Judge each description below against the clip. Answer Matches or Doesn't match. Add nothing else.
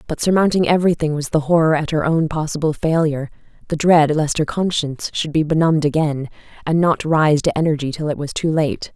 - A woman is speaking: Matches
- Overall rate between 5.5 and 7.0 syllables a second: Matches